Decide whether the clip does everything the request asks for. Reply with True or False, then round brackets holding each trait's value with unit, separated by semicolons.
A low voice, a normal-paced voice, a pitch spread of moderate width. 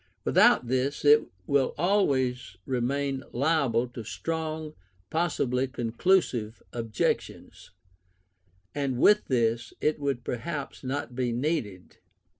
False (130 Hz; 100 wpm; 3.9 semitones)